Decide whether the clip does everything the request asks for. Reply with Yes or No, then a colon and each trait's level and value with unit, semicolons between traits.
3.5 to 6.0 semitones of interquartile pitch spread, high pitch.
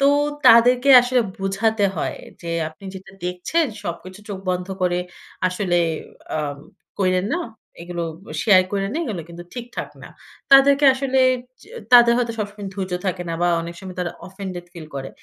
Yes: average, 4.9 semitones; high, 195 Hz